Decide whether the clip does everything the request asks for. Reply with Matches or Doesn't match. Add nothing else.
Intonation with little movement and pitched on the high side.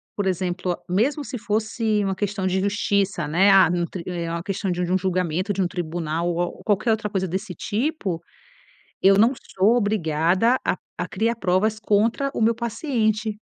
Doesn't match